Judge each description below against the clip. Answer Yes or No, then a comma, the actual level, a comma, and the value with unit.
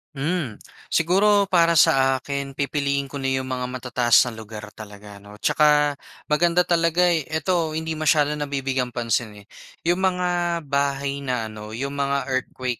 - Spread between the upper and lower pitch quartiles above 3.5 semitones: Yes, average, 4.3 semitones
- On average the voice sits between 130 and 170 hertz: Yes, medium, 140 Hz